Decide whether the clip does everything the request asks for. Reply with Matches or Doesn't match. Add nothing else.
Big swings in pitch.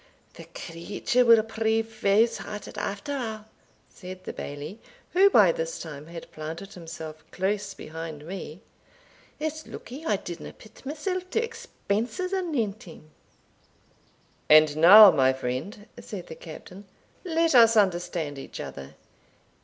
Matches